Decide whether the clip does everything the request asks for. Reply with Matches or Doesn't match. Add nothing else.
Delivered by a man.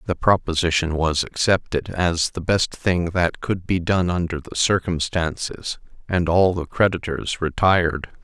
Matches